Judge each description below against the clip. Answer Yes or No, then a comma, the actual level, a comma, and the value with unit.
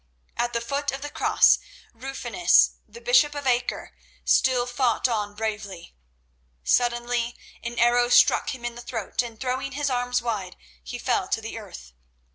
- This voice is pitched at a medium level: No, high, 240 Hz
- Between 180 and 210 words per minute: No, average, 155 wpm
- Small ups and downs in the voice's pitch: Yes, narrow, 2.0 semitones